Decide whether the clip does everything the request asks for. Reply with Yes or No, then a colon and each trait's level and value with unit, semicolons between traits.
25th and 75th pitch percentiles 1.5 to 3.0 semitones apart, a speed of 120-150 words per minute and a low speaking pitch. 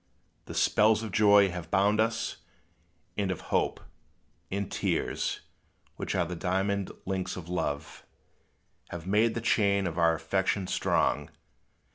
Yes: narrow, 2.5 semitones; slow, 135 wpm; very low, 95 Hz